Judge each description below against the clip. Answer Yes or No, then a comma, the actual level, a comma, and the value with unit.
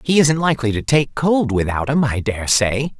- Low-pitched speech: Yes, low, 130 Hz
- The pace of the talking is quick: Yes, fast, 220 wpm